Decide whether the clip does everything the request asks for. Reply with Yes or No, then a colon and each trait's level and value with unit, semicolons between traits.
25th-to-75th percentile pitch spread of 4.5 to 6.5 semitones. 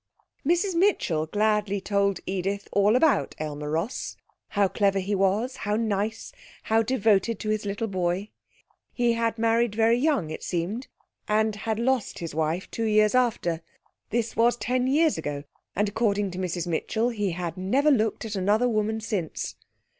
No: average, 3.3 semitones